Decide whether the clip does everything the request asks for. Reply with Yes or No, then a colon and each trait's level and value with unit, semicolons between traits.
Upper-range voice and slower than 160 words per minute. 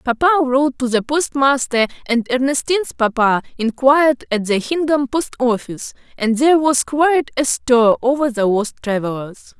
Yes: very high, 265 Hz; average, 150 wpm